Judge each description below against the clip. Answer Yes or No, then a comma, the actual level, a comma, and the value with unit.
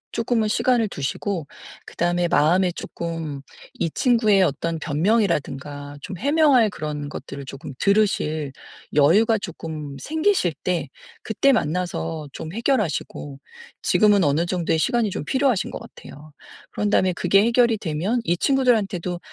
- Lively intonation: Yes, wide, 6.2 semitones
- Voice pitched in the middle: Yes, medium, 180 Hz